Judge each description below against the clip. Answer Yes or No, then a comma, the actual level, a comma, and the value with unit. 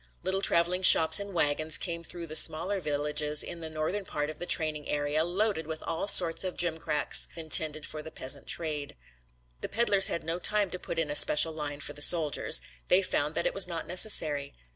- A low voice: No, medium, 160 Hz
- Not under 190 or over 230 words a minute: Yes, fast, 205 wpm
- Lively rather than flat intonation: No, average, 3.0 semitones